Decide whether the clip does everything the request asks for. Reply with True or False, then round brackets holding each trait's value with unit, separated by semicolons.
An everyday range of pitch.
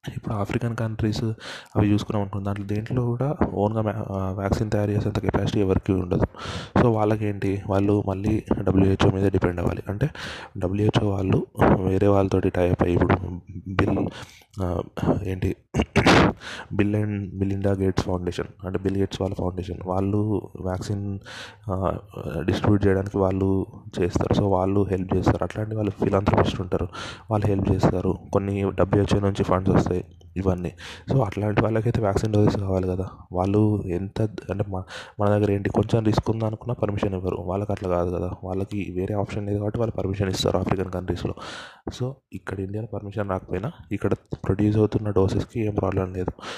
False (2.0 semitones)